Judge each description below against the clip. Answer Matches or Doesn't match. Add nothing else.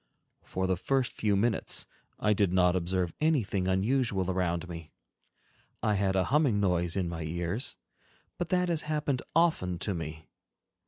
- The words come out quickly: Doesn't match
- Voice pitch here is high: Doesn't match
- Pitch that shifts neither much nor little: Doesn't match